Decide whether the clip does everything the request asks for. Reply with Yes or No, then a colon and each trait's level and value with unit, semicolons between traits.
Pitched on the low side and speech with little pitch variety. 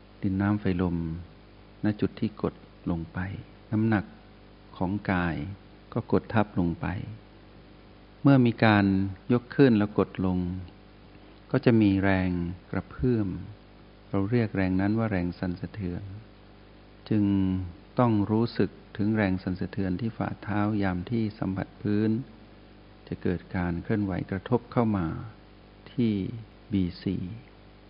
Yes: low, 105 Hz; narrow, 1.8 semitones